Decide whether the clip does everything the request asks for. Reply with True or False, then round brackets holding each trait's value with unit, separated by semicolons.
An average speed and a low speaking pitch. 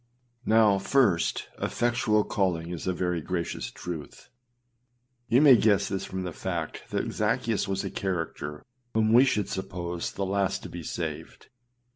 True (155 wpm; 95 Hz)